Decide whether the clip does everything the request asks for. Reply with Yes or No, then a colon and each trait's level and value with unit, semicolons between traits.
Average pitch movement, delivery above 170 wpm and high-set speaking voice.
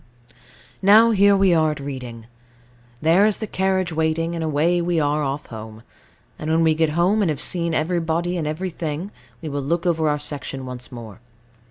No: average, 3.3 semitones; average, 185 wpm; medium, 160 Hz